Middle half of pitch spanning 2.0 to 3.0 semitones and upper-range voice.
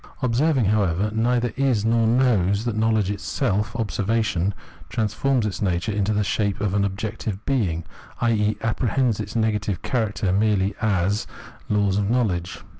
No: narrow, 2.4 semitones; low, 105 Hz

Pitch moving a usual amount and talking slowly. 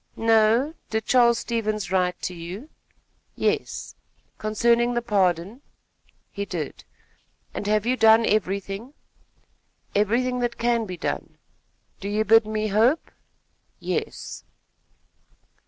Yes: average, 3.0 semitones; slow, 110 wpm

